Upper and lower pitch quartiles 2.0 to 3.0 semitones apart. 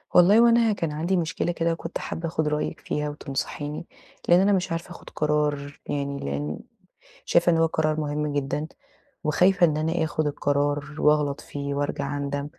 Yes: average, 2.7 semitones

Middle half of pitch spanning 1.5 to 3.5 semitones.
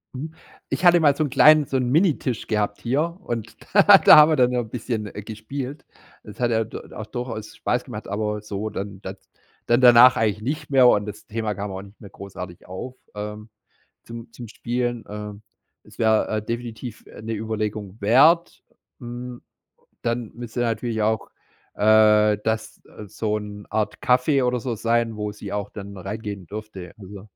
Yes: average, 2.8 semitones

